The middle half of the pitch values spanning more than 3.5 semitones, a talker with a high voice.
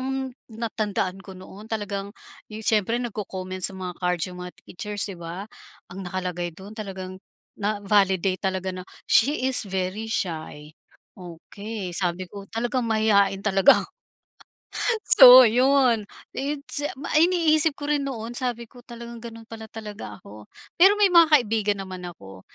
Yes: average, 4.1 semitones; high, 205 Hz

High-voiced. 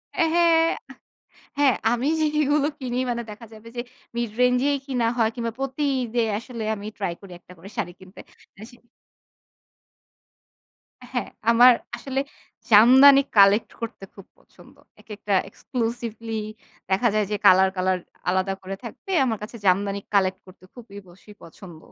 Yes: high, 225 Hz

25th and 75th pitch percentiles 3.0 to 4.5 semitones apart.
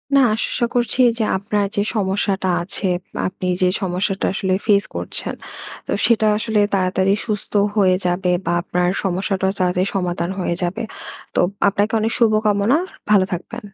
No: narrow, 2.5 semitones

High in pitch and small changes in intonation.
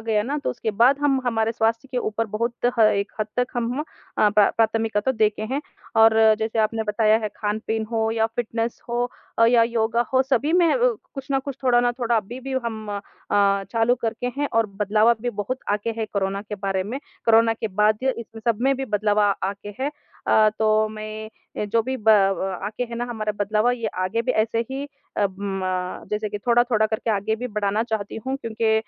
Yes: high, 220 Hz; narrow, 2.2 semitones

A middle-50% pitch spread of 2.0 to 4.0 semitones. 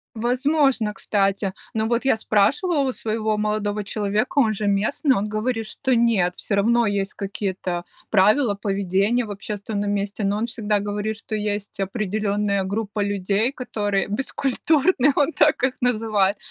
Yes: average, 2.9 semitones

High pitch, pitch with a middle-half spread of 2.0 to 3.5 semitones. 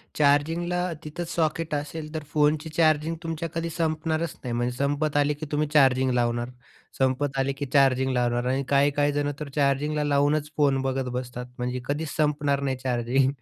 No: medium, 145 Hz; narrow, 2.6 semitones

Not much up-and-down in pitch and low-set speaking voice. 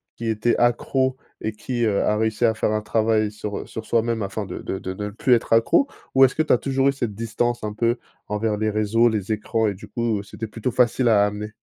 Yes: narrow, 2.0 semitones; low, 110 Hz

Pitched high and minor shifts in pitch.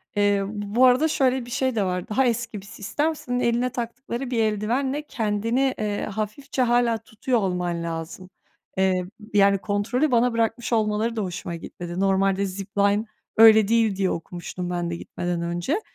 No: high, 215 Hz; average, 4.0 semitones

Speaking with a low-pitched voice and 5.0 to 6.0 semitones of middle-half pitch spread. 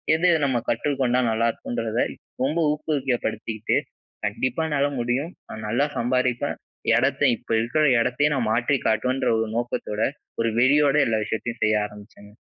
No: low, 120 Hz; average, 3.6 semitones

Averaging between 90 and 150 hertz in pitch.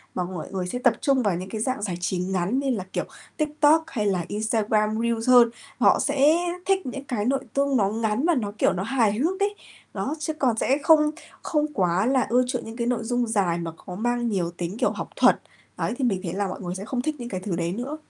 No: high, 230 Hz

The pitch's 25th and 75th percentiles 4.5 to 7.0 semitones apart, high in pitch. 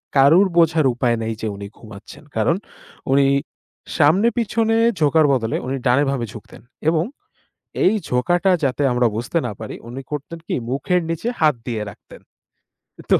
No: wide, 5.6 semitones; medium, 140 Hz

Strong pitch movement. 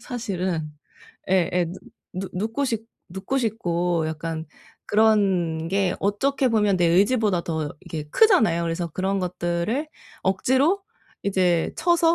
No: average, 4.6 semitones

